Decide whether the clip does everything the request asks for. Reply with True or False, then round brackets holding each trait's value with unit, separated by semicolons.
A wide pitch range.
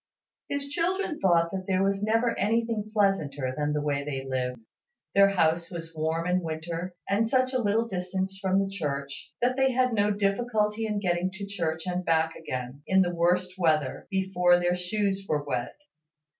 False (4.4 semitones)